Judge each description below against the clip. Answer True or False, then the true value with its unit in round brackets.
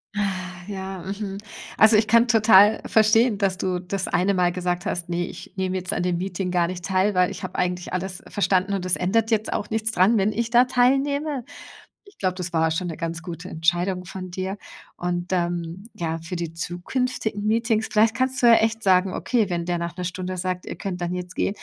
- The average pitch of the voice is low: False (185 Hz)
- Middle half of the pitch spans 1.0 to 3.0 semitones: False (3.4 semitones)